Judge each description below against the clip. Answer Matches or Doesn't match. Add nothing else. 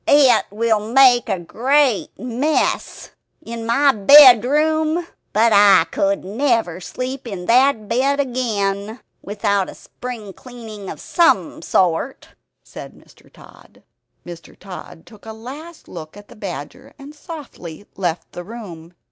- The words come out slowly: Matches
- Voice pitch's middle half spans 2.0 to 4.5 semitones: Doesn't match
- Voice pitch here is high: Matches